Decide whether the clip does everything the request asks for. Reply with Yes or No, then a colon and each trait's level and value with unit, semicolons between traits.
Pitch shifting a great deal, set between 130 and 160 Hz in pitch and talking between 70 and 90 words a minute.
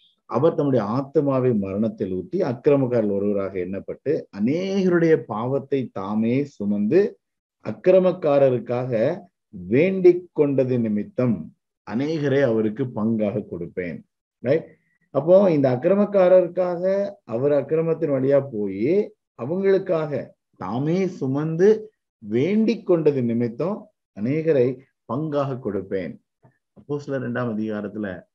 Yes: wide, 7.2 semitones; medium, 140 Hz; average, 85 wpm